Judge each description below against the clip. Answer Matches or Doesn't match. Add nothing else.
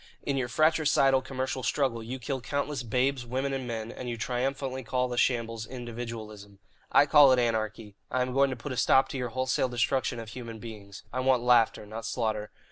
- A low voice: Matches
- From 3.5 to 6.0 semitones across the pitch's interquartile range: Doesn't match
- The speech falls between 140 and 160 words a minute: Doesn't match